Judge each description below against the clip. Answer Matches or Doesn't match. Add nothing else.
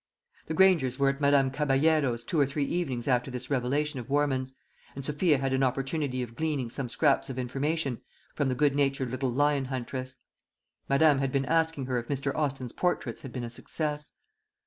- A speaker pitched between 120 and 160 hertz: Matches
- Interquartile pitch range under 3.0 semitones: Matches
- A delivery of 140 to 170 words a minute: Doesn't match